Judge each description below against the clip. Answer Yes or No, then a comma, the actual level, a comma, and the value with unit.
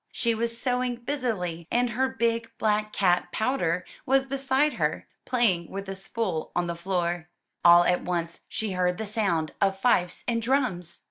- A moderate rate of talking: Yes, average, 165 wpm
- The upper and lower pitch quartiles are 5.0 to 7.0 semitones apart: Yes, wide, 5.4 semitones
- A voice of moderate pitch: No, high, 210 Hz